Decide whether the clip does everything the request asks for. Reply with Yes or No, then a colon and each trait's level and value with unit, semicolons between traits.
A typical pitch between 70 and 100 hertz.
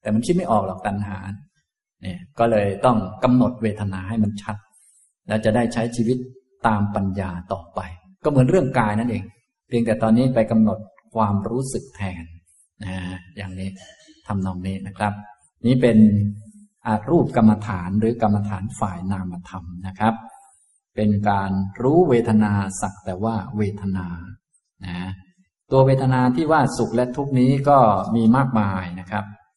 No: low, 110 Hz